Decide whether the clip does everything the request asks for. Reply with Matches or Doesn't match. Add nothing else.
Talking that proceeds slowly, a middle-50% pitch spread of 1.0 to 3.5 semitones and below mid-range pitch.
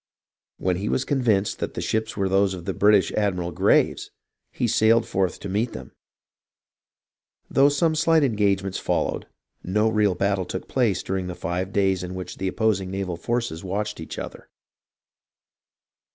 Doesn't match